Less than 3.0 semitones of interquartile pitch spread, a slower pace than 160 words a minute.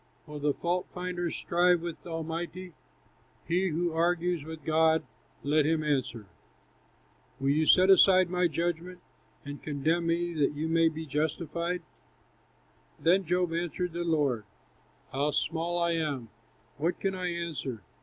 Yes: narrow, 2.4 semitones; average, 140 wpm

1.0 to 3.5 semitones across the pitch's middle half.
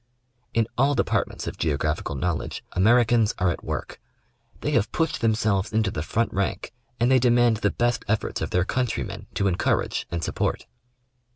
No: average, 4.7 semitones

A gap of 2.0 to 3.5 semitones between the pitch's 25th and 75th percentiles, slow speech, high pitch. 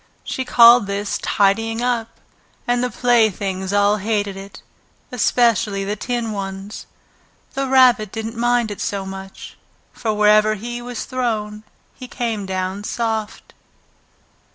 Yes: average, 3.1 semitones; slow, 130 wpm; high, 215 Hz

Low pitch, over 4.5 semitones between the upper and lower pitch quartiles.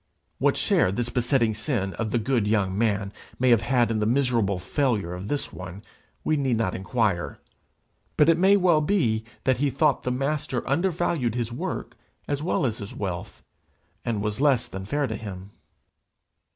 Yes: low, 120 Hz; average, 5.1 semitones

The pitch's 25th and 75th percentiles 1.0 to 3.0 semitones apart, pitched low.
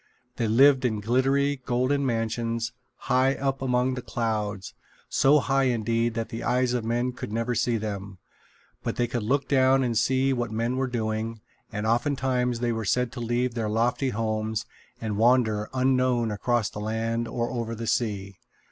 Yes: narrow, 2.4 semitones; low, 120 Hz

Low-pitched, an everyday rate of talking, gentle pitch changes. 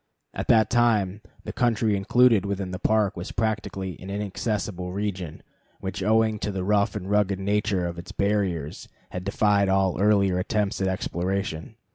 Yes: low, 100 Hz; average, 160 wpm; narrow, 2.1 semitones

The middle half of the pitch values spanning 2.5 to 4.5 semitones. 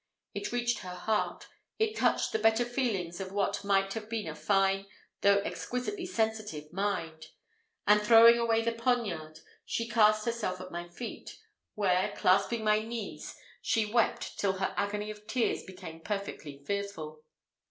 Yes: average, 3.4 semitones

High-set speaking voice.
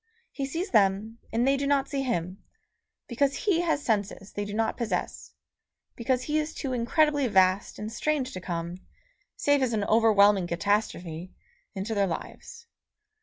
Yes: high, 225 Hz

